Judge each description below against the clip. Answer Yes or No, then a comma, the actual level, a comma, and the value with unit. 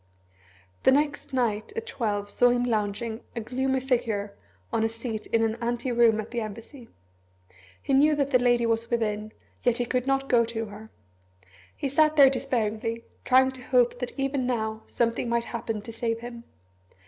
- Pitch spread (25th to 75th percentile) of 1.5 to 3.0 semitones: Yes, narrow, 2.5 semitones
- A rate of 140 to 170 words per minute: No, average, 180 wpm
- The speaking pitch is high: Yes, high, 235 Hz